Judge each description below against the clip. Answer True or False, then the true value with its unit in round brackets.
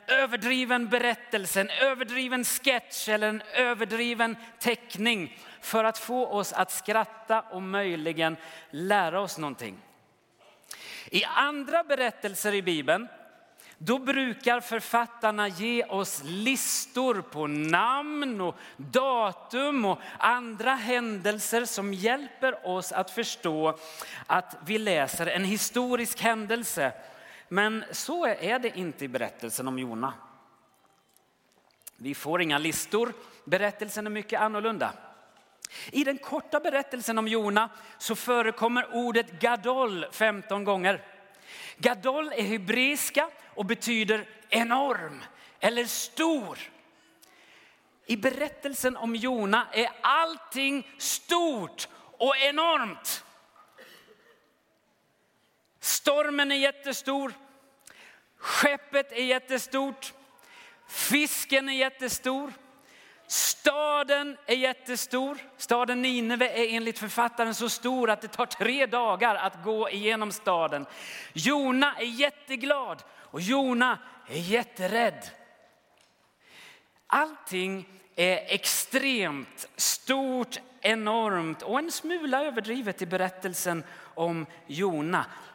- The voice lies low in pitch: False (235 Hz)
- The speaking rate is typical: False (100 wpm)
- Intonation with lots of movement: False (4.6 semitones)